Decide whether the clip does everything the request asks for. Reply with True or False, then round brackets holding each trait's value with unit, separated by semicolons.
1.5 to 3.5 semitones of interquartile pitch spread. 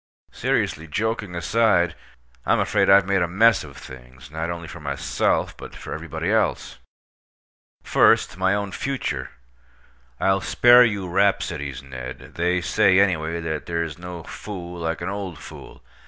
False (4.0 semitones)